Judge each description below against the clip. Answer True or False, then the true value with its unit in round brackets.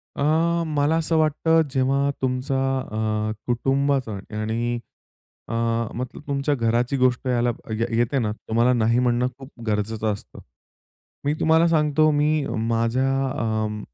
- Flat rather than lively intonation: False (3.7 semitones)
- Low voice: True (125 Hz)